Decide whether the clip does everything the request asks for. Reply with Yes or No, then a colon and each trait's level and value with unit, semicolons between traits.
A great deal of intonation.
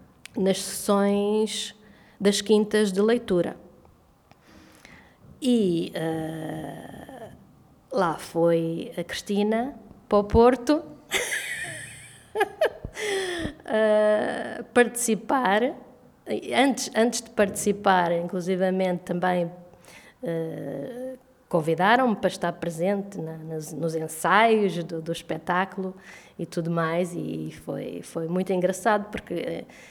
No: average, 4.3 semitones